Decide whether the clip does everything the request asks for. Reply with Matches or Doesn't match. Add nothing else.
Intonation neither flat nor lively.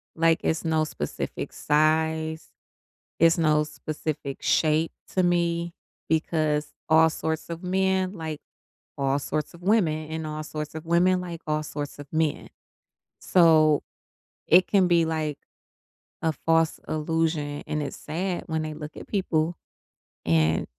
Doesn't match